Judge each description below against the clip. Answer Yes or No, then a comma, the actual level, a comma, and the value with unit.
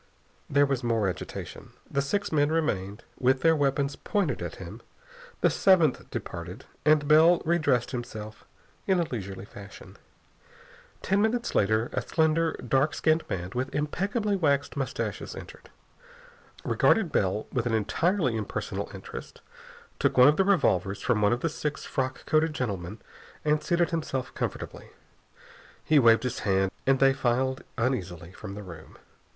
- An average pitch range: No, wide, 6.5 semitones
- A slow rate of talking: No, average, 150 wpm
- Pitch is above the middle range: No, low, 135 Hz